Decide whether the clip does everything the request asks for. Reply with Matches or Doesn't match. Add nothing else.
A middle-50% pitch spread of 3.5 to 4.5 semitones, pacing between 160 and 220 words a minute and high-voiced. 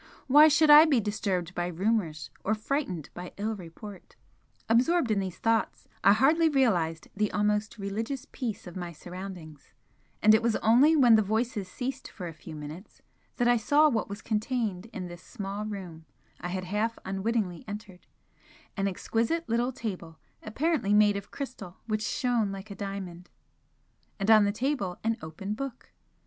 Matches